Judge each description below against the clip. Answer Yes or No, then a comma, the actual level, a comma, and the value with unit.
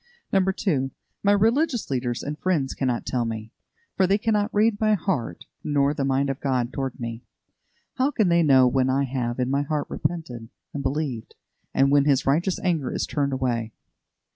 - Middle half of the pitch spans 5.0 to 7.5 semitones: Yes, wide, 5.5 semitones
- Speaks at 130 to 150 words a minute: No, average, 180 wpm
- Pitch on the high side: No, medium, 140 Hz